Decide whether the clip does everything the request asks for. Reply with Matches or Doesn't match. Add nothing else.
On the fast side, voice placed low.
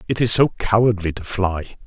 Doesn't match